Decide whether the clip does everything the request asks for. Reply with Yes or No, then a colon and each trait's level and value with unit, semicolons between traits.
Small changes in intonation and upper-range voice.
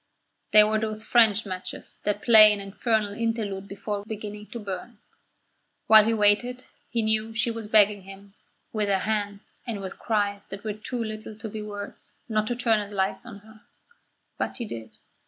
Yes: narrow, 1.4 semitones; high, 215 Hz